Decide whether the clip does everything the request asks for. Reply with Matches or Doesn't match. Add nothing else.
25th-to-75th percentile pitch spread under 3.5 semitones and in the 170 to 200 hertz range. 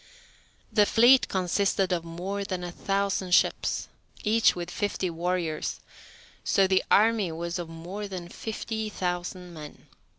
Matches